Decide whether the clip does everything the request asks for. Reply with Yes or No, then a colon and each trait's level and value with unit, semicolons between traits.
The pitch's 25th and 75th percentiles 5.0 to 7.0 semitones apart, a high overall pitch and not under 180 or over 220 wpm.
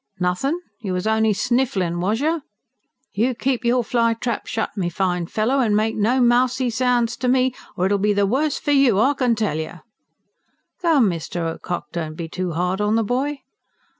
Yes: wide, 5.4 semitones; high, 225 Hz; average, 190 wpm